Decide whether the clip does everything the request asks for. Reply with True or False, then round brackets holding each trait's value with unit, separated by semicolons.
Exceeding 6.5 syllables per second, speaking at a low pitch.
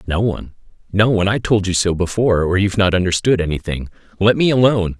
True (6.7 syllables/s; 100 Hz)